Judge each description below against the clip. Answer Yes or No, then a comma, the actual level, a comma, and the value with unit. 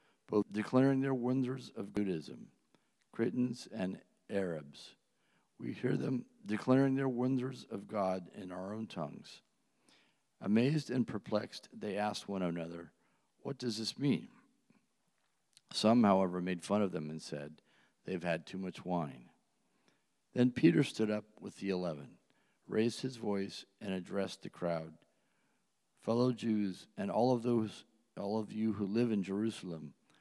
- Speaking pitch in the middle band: No, low, 105 Hz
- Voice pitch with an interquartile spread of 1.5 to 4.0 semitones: No, average, 4.9 semitones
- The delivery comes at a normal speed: Yes, average, 145 wpm